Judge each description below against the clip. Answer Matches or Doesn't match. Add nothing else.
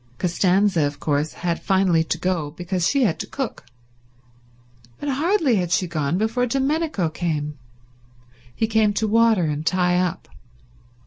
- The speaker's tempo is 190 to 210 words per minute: Doesn't match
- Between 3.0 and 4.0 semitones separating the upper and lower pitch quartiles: Doesn't match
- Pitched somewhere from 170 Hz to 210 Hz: Matches